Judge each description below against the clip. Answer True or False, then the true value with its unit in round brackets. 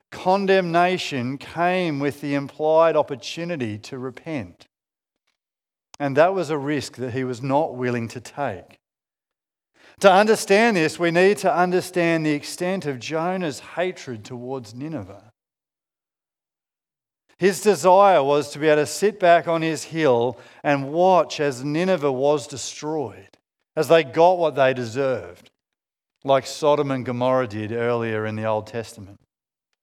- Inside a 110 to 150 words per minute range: True (135 wpm)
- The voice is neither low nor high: True (145 Hz)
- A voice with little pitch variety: False (5.1 semitones)